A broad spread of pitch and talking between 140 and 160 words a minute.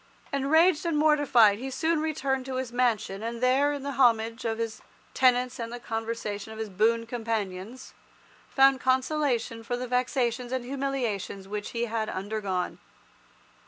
No: average, 3.1 semitones; average, 155 wpm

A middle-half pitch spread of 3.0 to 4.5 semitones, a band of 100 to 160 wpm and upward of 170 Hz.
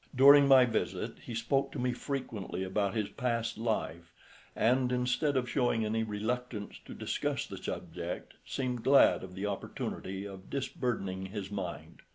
No: average, 4.2 semitones; average, 155 wpm; low, 115 Hz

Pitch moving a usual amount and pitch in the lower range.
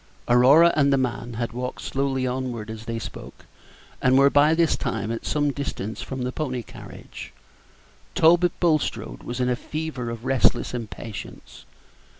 Yes: average, 3.5 semitones; low, 130 Hz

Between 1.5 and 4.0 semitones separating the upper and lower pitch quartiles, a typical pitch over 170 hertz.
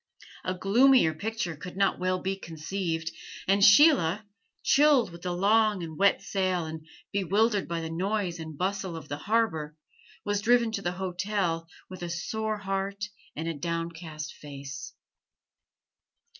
Yes: average, 3.7 semitones; medium, 185 Hz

